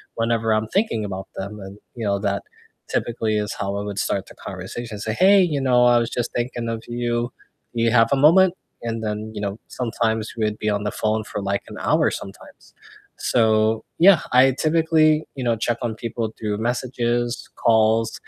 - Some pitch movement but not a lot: No, narrow, 2.3 semitones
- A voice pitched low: Yes, low, 115 Hz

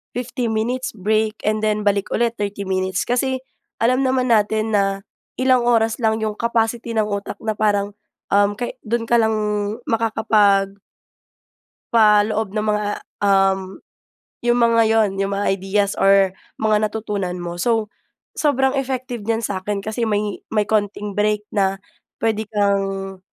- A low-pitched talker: No, high, 215 Hz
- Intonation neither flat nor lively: No, narrow, 2.2 semitones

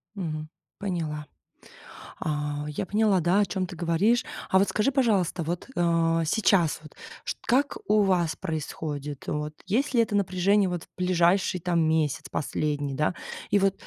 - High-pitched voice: No, medium, 175 Hz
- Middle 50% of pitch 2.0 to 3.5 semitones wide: No, average, 4.2 semitones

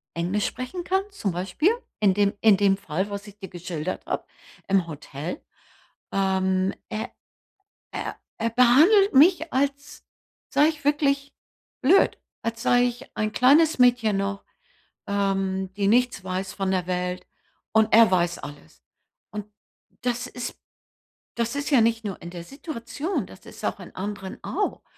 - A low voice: No, high, 210 Hz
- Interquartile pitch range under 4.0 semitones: No, average, 5.3 semitones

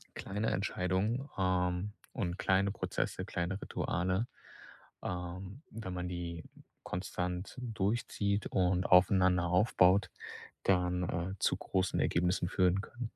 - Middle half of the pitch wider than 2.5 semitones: No, narrow, 2.0 semitones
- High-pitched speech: No, very low, 95 Hz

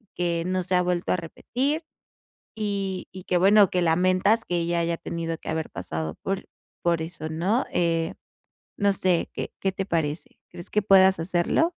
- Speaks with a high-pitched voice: No, medium, 180 Hz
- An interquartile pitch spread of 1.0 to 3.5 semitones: Yes, narrow, 2.6 semitones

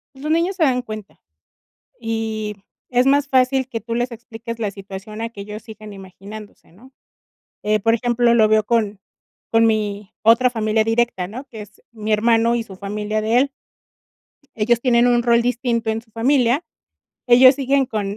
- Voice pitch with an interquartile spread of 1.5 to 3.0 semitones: Yes, narrow, 2.4 semitones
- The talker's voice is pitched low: No, high, 225 Hz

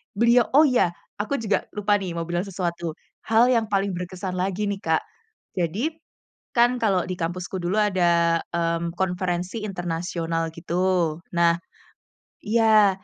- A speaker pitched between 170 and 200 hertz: Yes, medium, 185 Hz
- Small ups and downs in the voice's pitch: No, average, 3.4 semitones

